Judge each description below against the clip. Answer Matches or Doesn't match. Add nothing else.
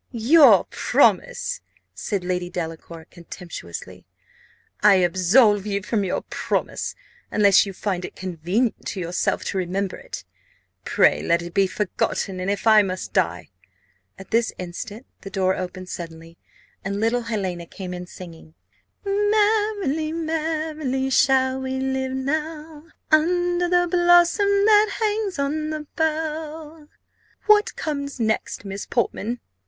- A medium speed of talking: Doesn't match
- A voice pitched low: Doesn't match